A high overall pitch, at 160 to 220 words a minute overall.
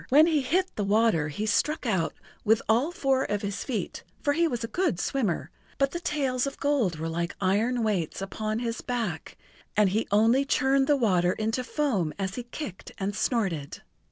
Yes: high, 225 Hz; average, 190 wpm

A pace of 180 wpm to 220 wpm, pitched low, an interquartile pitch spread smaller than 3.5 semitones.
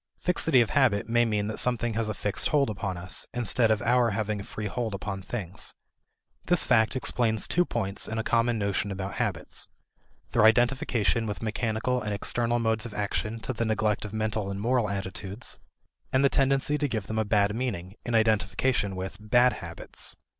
Yes: average, 190 wpm; low, 110 Hz; average, 2.9 semitones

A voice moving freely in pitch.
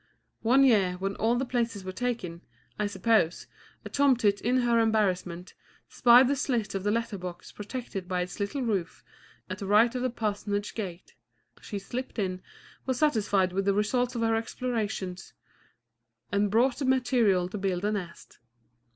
No: average, 4.1 semitones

